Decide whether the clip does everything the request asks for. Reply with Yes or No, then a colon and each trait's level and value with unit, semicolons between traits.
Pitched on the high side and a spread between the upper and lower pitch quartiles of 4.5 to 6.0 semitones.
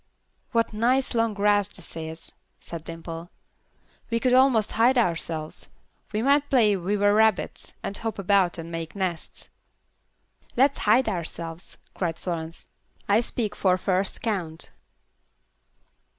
Yes: high, 200 Hz; average, 5.2 semitones